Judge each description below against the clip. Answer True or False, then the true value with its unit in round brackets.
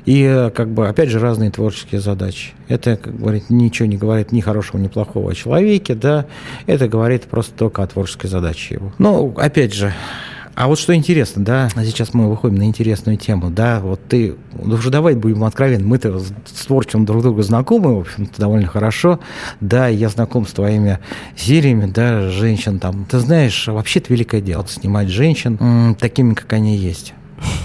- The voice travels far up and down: False (3.3 semitones)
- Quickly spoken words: True (175 wpm)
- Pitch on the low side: True (115 Hz)